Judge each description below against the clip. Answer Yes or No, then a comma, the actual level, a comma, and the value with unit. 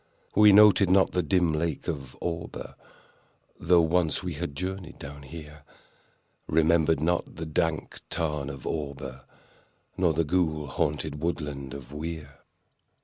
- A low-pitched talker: Yes, very low, 80 Hz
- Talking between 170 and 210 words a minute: No, average, 140 wpm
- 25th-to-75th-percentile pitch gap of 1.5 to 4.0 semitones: Yes, average, 2.9 semitones